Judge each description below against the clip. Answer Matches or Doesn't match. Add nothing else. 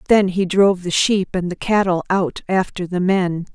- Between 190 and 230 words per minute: Matches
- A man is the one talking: Doesn't match